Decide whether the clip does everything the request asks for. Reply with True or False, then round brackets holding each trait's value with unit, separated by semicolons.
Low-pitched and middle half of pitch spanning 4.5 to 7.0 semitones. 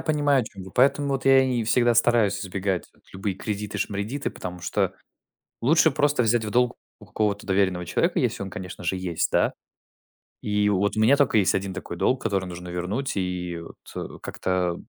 True (105 Hz; 4.9 semitones)